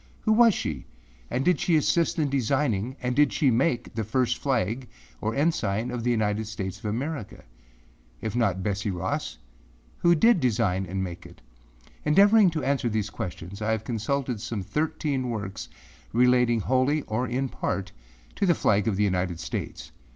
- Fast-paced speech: No, average, 170 wpm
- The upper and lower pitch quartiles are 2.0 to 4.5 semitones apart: No, average, 5.2 semitones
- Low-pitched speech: Yes, low, 120 Hz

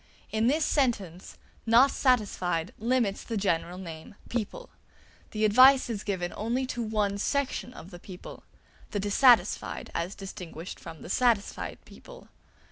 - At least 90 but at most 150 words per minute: Yes, slow, 135 wpm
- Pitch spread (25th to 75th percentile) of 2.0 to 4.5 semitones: No, average, 5.0 semitones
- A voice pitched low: No, high, 215 Hz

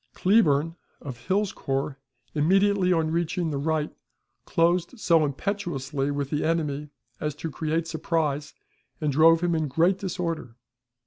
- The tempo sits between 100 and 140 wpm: Yes, slow, 135 wpm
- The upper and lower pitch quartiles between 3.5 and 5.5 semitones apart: No, average, 3.1 semitones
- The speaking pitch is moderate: Yes, medium, 160 Hz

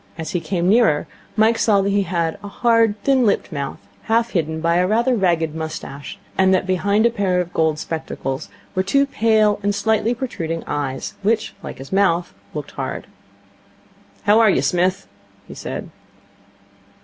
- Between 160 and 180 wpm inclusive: Yes, average, 170 wpm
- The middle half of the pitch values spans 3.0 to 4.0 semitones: No, average, 4.8 semitones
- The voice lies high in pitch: Yes, high, 195 Hz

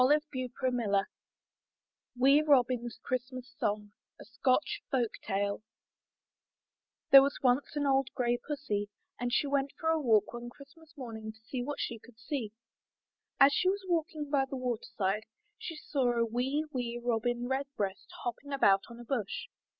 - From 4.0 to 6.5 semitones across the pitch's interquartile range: No, average, 3.2 semitones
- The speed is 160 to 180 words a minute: Yes, average, 165 wpm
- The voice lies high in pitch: Yes, very high, 250 Hz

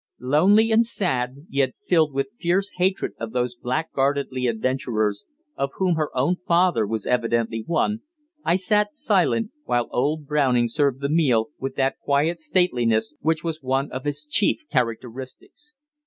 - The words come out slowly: No, average, 150 wpm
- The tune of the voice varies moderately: No, wide, 5.7 semitones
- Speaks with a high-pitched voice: No, medium, 140 Hz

